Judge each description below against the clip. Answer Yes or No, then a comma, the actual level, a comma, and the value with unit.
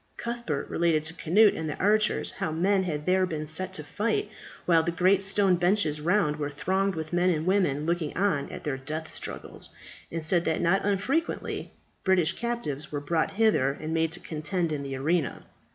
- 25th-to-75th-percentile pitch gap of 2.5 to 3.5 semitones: No, average, 3.9 semitones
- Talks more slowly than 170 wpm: No, average, 190 wpm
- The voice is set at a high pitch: No, medium, 170 Hz